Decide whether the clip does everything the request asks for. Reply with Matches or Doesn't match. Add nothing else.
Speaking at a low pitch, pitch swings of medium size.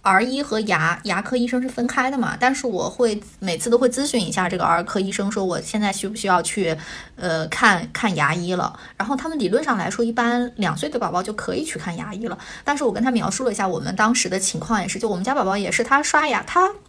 Doesn't match